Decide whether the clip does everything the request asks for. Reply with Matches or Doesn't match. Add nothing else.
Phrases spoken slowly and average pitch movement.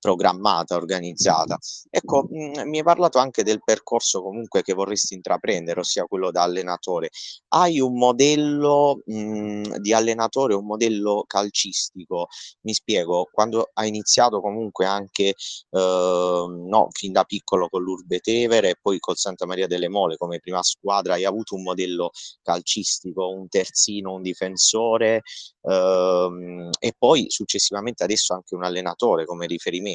Doesn't match